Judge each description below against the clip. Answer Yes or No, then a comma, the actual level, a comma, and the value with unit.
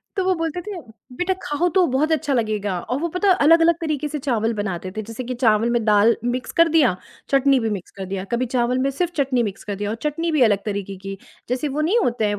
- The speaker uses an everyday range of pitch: No, wide, 6.8 semitones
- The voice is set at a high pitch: Yes, very high, 255 Hz